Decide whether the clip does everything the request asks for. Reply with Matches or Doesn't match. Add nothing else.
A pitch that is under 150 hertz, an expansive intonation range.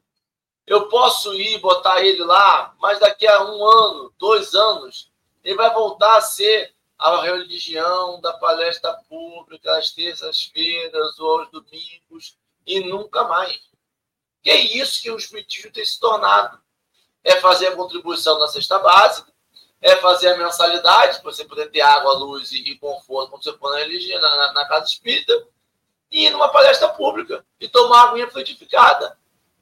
Doesn't match